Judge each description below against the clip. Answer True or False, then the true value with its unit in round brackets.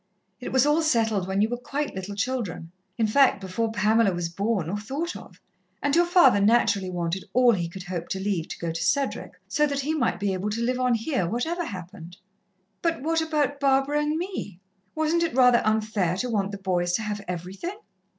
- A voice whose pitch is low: False (220 Hz)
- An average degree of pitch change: False (6.7 semitones)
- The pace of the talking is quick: True (210 wpm)